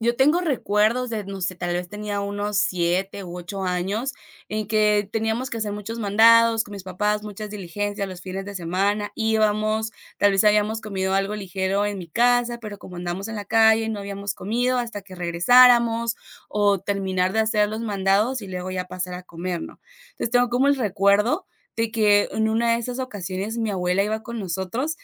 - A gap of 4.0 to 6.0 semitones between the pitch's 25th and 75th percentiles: No, average, 2.7 semitones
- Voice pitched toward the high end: Yes, high, 205 Hz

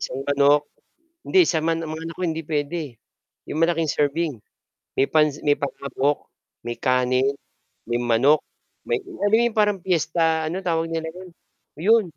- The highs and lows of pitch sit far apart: No, average, 3.1 semitones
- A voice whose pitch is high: No, medium, 160 Hz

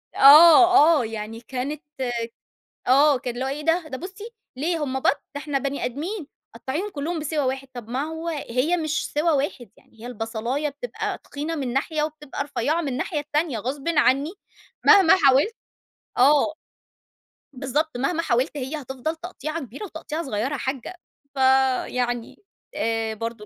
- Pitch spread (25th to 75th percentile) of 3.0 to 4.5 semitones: Yes, average, 3.7 semitones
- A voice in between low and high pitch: No, very high, 280 Hz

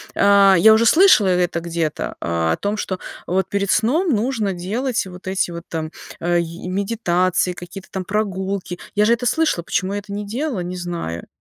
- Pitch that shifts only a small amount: No, average, 3.2 semitones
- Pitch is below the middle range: No, high, 190 Hz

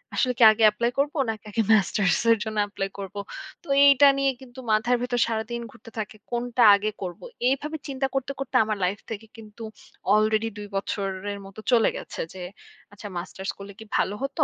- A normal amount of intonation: Yes, average, 3.3 semitones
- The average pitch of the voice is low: No, high, 220 Hz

